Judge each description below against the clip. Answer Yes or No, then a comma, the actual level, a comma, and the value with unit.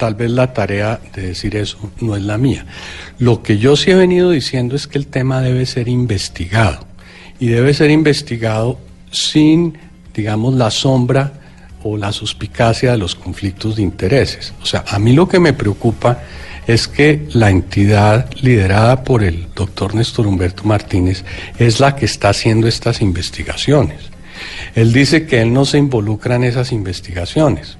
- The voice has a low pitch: Yes, low, 115 Hz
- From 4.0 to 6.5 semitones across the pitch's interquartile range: Yes, average, 4.5 semitones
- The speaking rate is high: No, average, 165 wpm